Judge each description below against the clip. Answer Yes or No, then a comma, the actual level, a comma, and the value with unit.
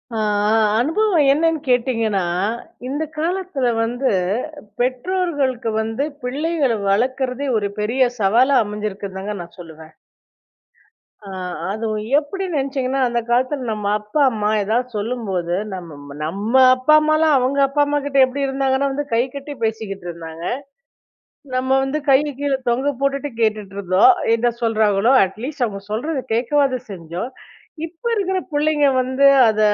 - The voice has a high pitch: Yes, very high, 250 Hz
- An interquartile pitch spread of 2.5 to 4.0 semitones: No, average, 5.2 semitones